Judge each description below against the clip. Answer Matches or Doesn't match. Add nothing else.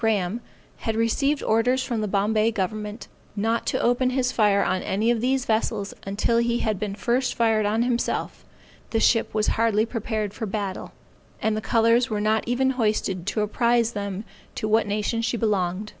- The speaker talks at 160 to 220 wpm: Matches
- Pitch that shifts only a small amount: Matches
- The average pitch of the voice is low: Doesn't match